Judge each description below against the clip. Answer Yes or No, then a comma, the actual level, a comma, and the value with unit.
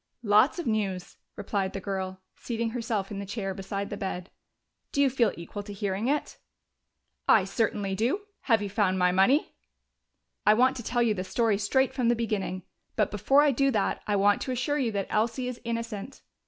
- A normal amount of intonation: Yes, average, 3.5 semitones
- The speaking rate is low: No, average, 195 wpm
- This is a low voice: No, high, 210 Hz